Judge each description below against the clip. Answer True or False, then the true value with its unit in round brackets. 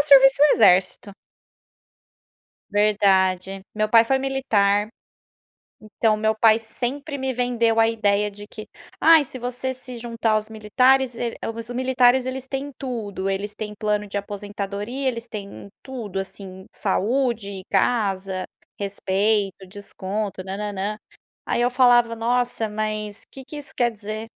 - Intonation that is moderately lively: True (3.5 semitones)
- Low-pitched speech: False (215 Hz)